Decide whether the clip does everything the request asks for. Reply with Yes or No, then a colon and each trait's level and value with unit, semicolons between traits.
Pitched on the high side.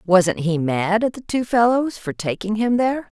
Yes: high, 210 Hz